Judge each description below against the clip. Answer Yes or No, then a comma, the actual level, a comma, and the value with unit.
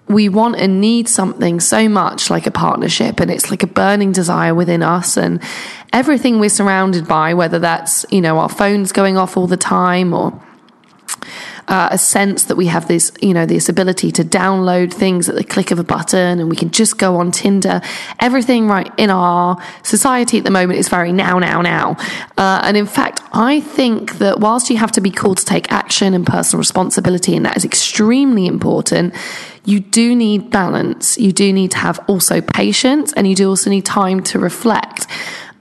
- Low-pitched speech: No, high, 195 Hz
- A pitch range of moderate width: Yes, average, 3.1 semitones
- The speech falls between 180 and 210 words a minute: Yes, average, 200 wpm